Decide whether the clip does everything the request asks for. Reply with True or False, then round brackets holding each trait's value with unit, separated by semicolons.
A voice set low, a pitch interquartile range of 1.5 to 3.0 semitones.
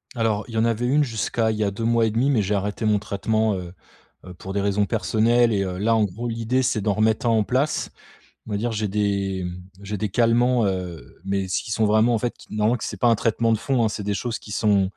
True (110 Hz; 2.4 semitones)